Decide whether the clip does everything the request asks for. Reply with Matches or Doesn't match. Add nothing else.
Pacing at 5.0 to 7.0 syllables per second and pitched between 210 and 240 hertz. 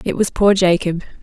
Doesn't match